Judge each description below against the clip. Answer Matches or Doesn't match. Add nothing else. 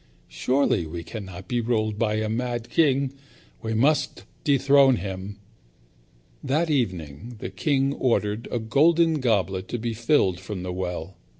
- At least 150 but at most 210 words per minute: Doesn't match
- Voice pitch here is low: Matches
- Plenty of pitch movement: Matches